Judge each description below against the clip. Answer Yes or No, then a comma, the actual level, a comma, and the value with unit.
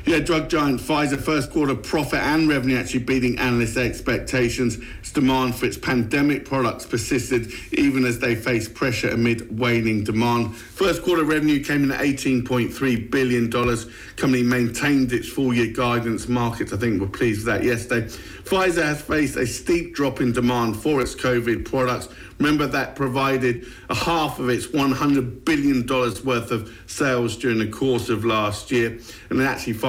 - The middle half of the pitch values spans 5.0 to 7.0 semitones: No, average, 2.7 semitones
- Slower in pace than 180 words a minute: Yes, average, 165 wpm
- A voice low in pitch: Yes, low, 125 Hz